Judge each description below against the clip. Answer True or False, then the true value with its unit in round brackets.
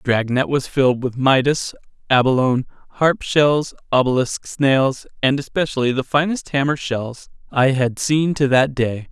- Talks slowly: False (150 wpm)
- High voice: False (135 Hz)